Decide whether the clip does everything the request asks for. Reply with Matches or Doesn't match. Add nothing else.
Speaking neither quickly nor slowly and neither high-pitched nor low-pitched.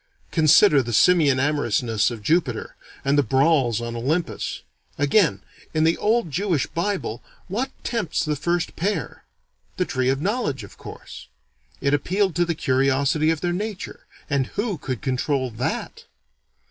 Matches